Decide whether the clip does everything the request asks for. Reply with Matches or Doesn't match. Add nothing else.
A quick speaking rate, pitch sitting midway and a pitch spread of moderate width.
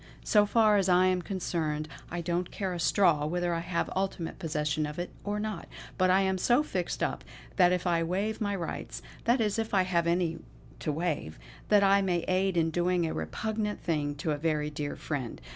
Matches